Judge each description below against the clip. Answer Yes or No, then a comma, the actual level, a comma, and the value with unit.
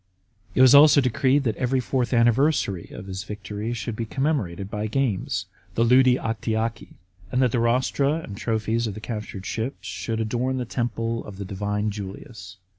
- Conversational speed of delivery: Yes, average, 170 wpm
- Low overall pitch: Yes, low, 115 Hz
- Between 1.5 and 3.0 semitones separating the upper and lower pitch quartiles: No, average, 3.5 semitones